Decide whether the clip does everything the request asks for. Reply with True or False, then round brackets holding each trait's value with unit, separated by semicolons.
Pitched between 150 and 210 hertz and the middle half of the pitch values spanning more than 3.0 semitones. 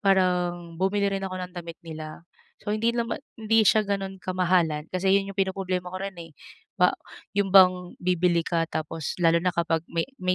False (185 Hz; 2.5 semitones)